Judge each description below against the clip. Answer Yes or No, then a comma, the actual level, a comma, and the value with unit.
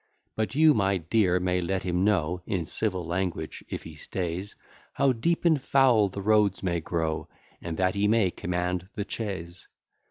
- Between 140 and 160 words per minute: No, average, 170 wpm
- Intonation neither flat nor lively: Yes, average, 3.5 semitones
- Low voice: Yes, very low, 95 Hz